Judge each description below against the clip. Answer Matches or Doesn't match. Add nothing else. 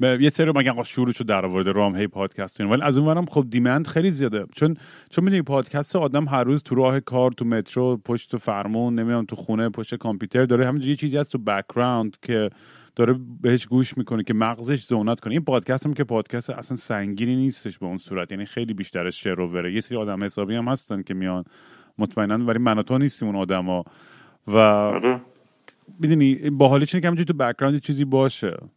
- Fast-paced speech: Matches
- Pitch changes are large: Doesn't match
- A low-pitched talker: Matches